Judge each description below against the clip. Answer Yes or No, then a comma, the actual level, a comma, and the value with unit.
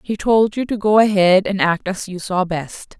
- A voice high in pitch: Yes, high, 195 Hz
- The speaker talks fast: Yes, fast, 240 wpm